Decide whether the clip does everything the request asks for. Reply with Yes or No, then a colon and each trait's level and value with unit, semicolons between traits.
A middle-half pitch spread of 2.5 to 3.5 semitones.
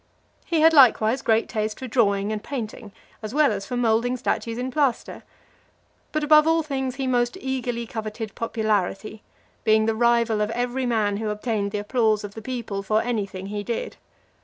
Yes: average, 3.0 semitones